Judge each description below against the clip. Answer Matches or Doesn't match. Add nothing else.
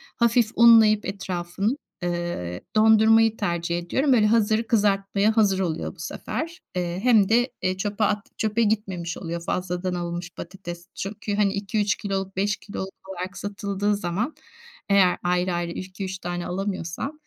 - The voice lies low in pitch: Doesn't match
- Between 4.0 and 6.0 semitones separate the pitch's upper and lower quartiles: Doesn't match